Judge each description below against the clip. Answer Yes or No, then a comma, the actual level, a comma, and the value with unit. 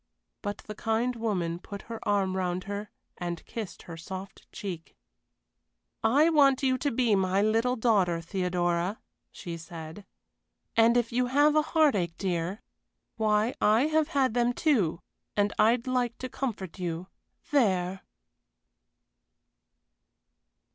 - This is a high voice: Yes, high, 210 Hz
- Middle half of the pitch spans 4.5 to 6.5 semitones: Yes, average, 5.2 semitones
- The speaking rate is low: Yes, slow, 130 wpm